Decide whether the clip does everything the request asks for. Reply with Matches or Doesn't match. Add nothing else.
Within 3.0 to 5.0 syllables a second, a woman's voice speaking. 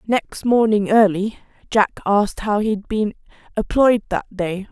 Matches